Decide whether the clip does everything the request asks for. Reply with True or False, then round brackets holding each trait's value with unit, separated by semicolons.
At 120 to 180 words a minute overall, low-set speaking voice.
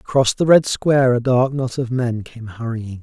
False (220 wpm; 125 Hz)